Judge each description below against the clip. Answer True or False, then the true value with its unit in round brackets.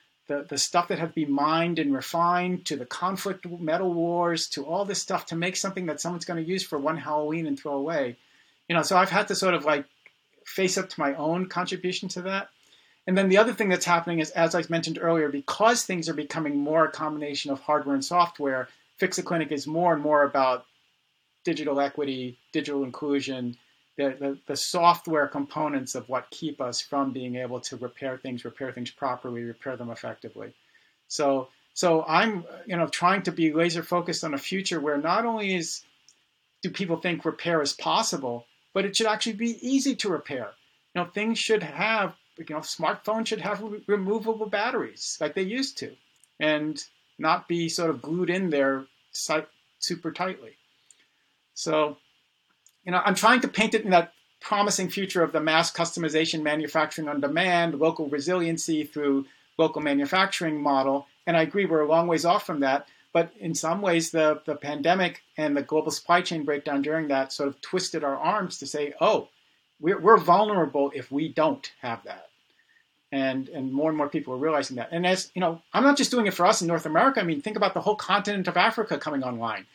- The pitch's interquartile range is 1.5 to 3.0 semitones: False (3.8 semitones)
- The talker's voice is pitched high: False (160 Hz)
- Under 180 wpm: False (195 wpm)